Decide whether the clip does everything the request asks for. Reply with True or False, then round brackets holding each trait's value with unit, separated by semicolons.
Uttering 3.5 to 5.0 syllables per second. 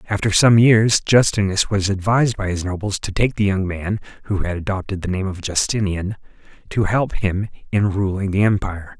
False (5.3 syllables/s)